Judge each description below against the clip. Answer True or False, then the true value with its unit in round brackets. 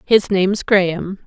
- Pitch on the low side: False (190 Hz)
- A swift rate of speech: False (140 wpm)